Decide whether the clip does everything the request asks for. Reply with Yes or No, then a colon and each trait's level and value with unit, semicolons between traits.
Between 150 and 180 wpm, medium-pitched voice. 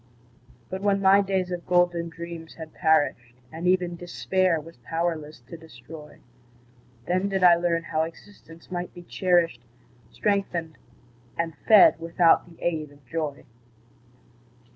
No: slow, 135 wpm; medium, 170 Hz